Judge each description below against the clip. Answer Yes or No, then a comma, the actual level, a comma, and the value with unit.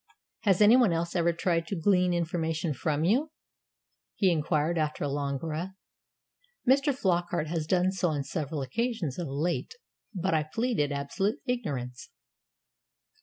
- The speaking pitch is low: No, medium, 170 Hz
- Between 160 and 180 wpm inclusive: No, average, 140 wpm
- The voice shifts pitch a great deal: No, average, 4.1 semitones